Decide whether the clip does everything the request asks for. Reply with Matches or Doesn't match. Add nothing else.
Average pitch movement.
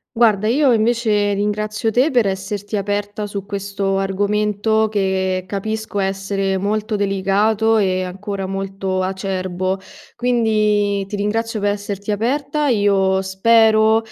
Doesn't match